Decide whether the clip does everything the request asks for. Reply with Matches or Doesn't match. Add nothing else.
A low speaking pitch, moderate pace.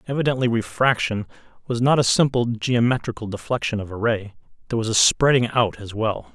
Matches